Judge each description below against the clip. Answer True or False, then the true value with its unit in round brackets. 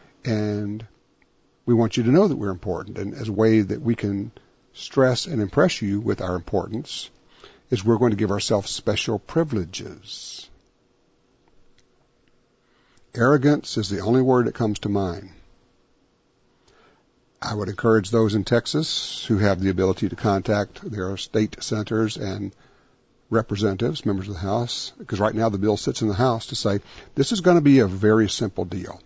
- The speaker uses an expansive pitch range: False (3.1 semitones)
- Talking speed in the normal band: True (165 wpm)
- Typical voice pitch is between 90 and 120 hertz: True (110 Hz)